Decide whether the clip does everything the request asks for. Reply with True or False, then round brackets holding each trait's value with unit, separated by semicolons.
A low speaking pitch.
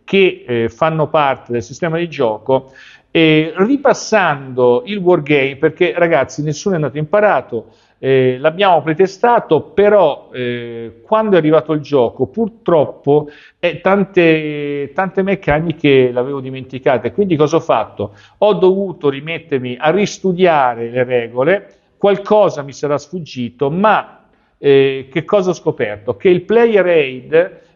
False (155 Hz)